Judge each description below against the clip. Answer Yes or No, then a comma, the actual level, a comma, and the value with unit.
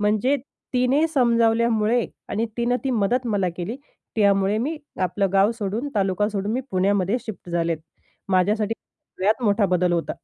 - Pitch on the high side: Yes, high, 210 Hz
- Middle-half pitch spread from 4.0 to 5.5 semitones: No, average, 3.3 semitones